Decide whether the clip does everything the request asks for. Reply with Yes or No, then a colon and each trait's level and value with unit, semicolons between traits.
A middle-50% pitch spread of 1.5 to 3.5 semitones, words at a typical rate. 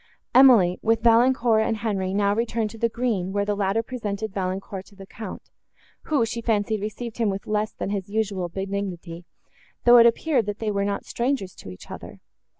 Yes: average, 2.9 semitones; average, 190 wpm